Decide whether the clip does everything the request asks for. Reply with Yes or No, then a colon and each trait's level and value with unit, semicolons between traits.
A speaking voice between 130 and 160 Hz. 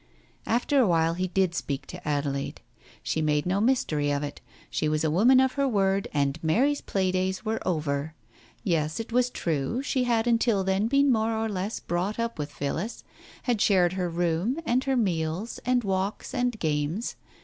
No: high, 190 Hz